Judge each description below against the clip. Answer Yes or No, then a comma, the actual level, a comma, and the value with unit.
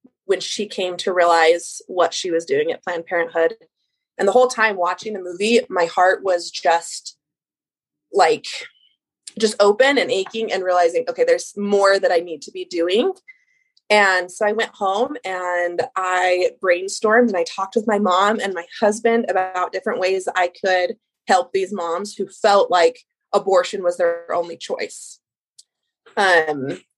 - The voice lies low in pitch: No, high, 200 Hz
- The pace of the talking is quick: No, average, 160 wpm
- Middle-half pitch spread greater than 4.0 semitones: Yes, average, 5.2 semitones